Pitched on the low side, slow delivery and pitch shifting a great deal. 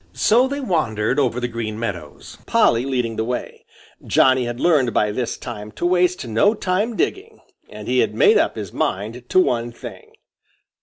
No: low, 125 Hz; average, 175 wpm; wide, 8.1 semitones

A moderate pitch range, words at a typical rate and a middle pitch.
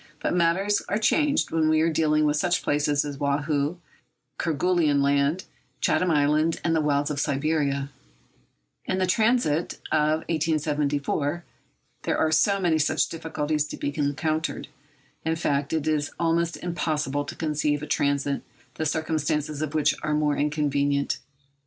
No: narrow, 2.1 semitones; average, 145 wpm; medium, 155 Hz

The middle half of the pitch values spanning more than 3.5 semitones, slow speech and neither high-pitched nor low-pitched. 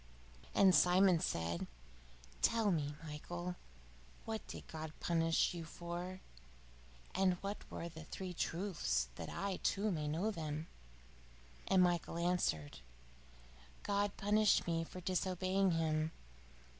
No: average, 3.2 semitones; slow, 120 wpm; medium, 175 Hz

